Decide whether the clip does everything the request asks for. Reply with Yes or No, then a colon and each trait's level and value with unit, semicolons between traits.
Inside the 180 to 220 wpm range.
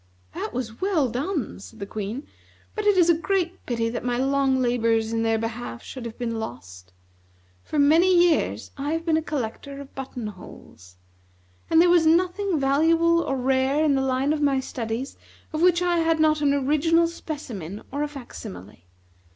Yes: average, 185 wpm